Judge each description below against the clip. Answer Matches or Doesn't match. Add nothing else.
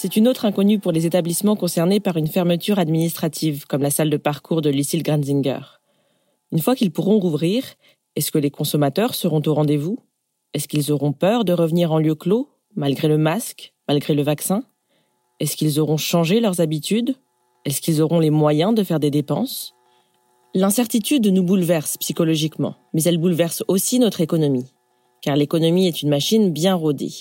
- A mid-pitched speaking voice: Matches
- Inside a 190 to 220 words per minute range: Doesn't match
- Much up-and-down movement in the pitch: Doesn't match